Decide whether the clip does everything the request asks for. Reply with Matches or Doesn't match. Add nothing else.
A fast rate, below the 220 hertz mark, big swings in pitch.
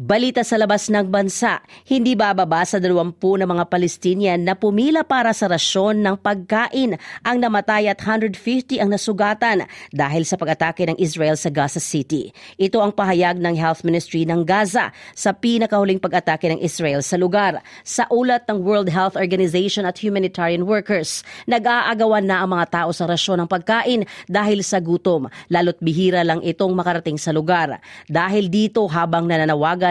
Doesn't match